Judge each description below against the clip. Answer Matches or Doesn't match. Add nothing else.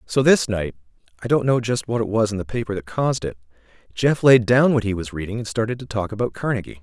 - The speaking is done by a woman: Doesn't match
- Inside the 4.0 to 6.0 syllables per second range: Doesn't match